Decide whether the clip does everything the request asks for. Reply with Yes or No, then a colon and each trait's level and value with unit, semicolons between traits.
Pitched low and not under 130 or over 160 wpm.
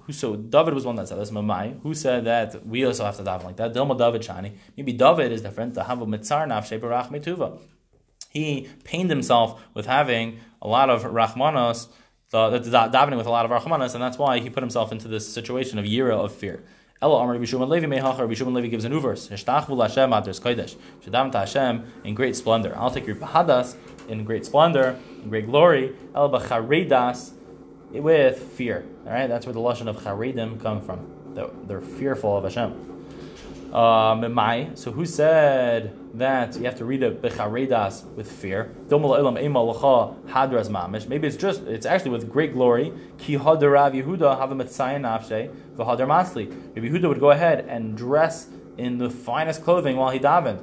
Yes: low, 120 Hz; average, 140 wpm